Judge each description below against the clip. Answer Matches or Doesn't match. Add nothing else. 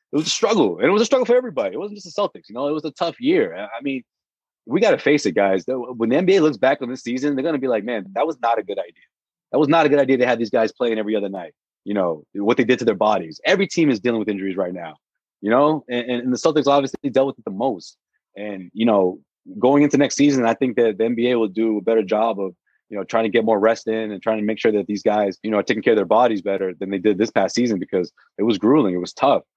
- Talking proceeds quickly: Matches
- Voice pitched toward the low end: Matches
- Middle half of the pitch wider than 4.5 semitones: Matches